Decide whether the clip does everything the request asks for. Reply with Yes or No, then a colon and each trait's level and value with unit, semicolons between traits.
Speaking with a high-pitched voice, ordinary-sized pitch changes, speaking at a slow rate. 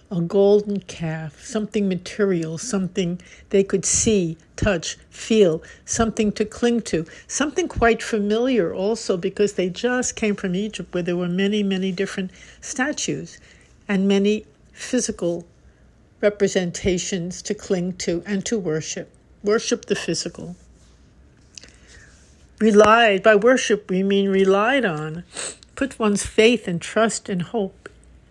Yes: high, 200 Hz; average, 3.0 semitones; slow, 125 wpm